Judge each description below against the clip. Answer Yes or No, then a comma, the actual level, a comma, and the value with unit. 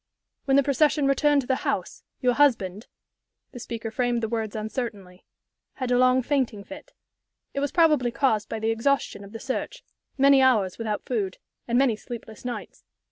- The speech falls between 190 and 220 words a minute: No, average, 175 wpm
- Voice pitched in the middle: No, high, 245 Hz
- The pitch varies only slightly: No, average, 3.8 semitones